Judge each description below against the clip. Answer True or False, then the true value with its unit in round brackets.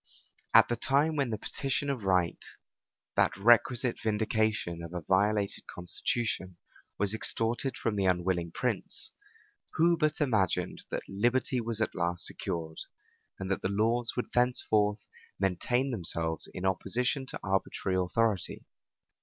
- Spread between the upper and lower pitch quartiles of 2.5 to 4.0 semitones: False (4.7 semitones)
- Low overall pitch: True (105 Hz)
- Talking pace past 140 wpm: False (135 wpm)